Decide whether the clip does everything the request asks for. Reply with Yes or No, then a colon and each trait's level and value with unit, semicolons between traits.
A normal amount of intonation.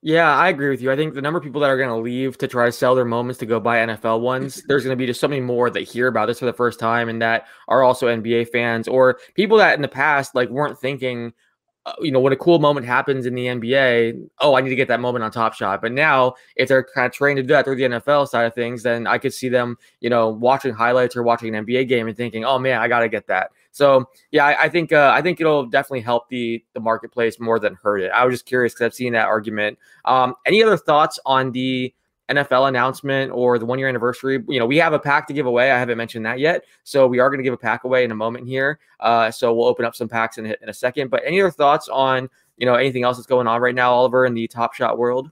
No: narrow, 2.3 semitones